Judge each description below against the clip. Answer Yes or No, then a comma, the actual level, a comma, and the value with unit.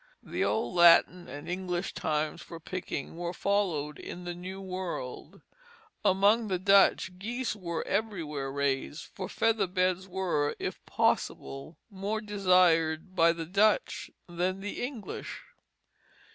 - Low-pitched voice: No, medium, 180 Hz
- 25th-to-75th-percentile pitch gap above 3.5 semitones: No, average, 3.1 semitones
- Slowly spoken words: Yes, slow, 130 wpm